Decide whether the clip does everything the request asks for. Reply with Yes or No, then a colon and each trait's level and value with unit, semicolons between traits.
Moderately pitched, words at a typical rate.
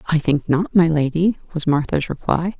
Yes: medium, 160 Hz; average, 185 wpm